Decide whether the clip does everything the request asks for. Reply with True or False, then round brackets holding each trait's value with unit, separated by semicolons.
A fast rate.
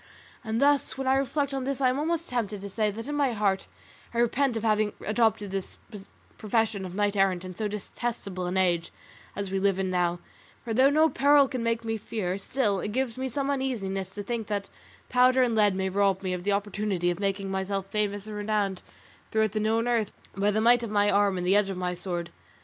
True (225 wpm)